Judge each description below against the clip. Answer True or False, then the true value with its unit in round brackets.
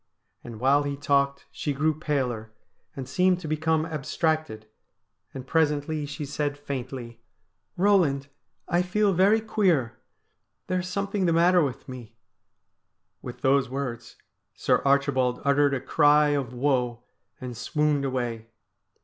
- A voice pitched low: False (145 Hz)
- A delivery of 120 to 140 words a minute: True (135 wpm)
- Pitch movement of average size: True (3.6 semitones)